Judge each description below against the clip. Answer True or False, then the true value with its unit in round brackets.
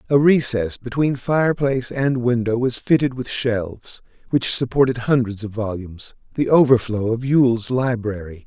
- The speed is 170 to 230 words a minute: False (140 wpm)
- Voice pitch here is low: True (120 Hz)